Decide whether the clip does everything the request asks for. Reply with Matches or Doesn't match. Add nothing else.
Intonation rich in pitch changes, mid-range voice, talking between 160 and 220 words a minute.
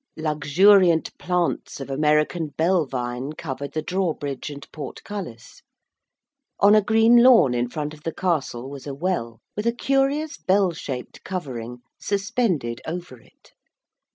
Doesn't match